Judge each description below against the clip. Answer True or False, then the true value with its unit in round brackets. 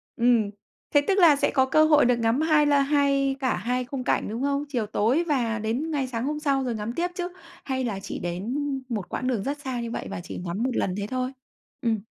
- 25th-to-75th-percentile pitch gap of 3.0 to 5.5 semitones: True (3.9 semitones)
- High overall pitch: True (255 Hz)